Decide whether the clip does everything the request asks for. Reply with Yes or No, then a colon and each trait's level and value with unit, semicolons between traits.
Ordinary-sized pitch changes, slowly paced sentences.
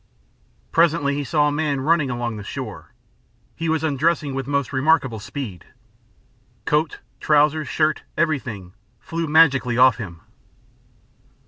Yes: average, 3.8 semitones; slow, 125 wpm